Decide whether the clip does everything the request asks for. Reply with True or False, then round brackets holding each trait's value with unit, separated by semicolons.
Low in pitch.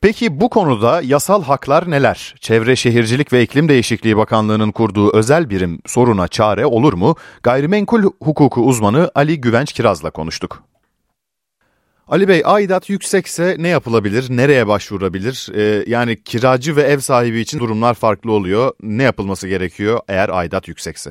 True (120 Hz)